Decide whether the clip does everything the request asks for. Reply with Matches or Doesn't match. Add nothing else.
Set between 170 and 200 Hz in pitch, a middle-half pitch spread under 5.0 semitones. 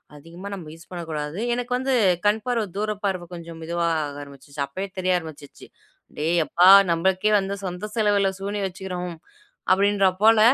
Matches